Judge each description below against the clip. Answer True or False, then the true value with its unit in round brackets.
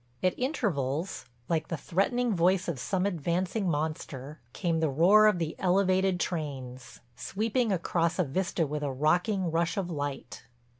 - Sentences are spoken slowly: False (150 wpm)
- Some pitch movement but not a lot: True (4.0 semitones)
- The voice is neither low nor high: True (170 Hz)